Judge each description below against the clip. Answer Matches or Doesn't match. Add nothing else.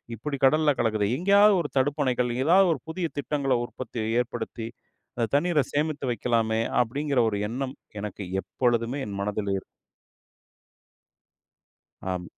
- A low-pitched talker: Matches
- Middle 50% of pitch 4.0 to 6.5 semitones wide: Matches